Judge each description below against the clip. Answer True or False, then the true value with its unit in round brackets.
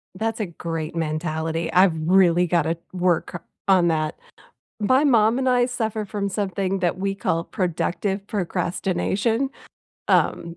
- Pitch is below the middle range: False (185 Hz)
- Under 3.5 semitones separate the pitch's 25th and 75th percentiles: False (3.8 semitones)